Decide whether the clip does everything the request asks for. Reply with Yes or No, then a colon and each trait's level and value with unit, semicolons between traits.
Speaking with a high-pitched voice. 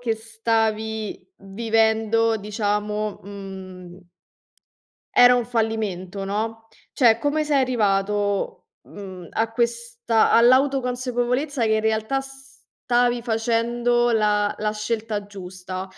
Yes: high, 225 Hz